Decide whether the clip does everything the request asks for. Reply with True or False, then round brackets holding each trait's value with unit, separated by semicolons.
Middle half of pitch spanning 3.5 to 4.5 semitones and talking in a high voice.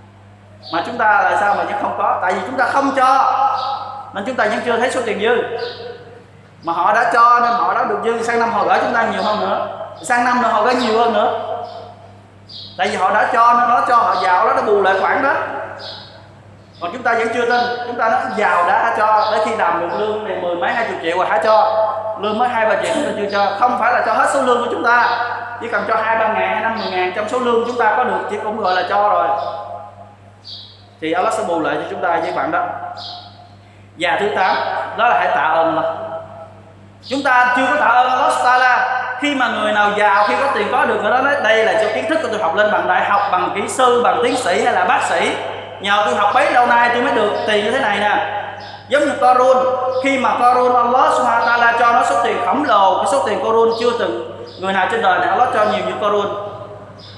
True (4.1 semitones; 225 Hz)